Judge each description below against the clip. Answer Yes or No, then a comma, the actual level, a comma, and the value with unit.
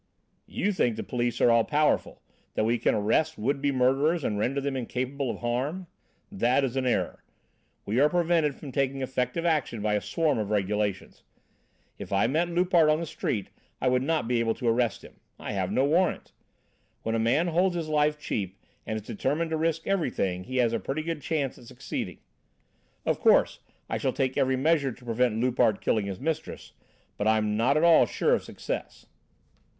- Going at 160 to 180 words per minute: No, average, 195 wpm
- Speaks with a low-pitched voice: Yes, low, 130 Hz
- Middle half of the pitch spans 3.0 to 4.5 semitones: No, average, 5.3 semitones